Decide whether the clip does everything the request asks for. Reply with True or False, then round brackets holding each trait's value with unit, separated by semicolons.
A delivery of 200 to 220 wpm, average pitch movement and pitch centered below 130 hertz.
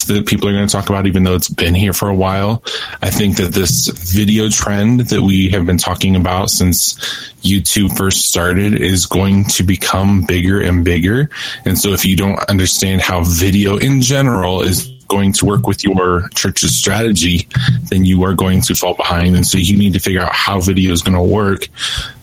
False (205 wpm; 1.9 semitones; 95 Hz)